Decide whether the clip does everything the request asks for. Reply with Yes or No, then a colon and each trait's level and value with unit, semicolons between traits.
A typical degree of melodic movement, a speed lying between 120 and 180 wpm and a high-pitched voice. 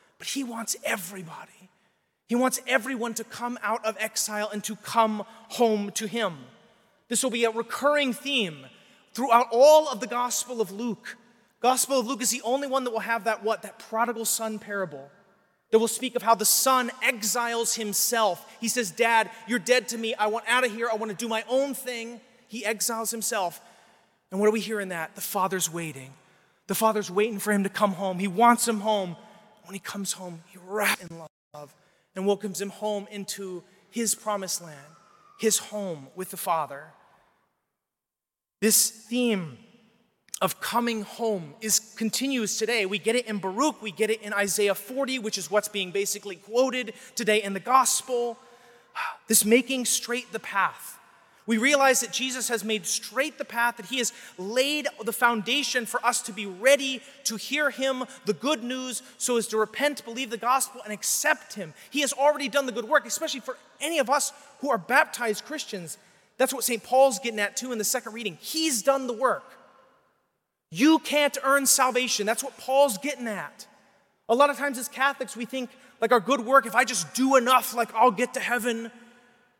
No: average, 3.5 semitones; average, 190 wpm; high, 230 Hz